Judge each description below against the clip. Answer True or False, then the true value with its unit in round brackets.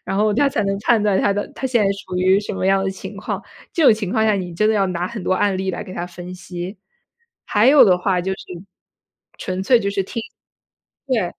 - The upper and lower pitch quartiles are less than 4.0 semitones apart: True (2.6 semitones)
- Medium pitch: False (195 Hz)